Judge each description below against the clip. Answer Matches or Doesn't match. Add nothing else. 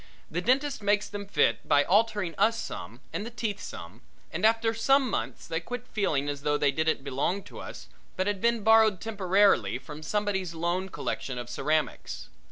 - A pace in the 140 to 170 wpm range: Doesn't match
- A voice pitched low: Doesn't match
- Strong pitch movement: Matches